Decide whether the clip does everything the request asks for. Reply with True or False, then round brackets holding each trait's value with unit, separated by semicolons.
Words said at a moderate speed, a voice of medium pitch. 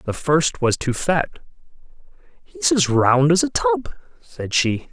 True (160 wpm; 145 Hz)